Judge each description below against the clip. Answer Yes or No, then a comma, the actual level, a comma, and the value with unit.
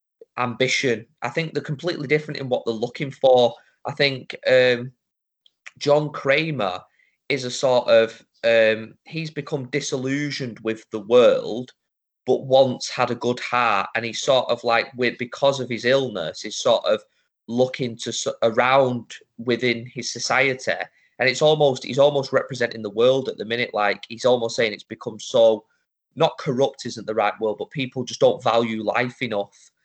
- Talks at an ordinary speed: Yes, average, 165 wpm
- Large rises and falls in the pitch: No, average, 2.9 semitones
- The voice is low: Yes, low, 125 Hz